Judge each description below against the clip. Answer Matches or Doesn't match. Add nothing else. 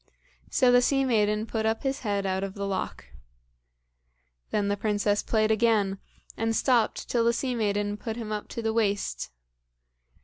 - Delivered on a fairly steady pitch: Matches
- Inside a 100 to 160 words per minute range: Doesn't match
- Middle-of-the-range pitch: Doesn't match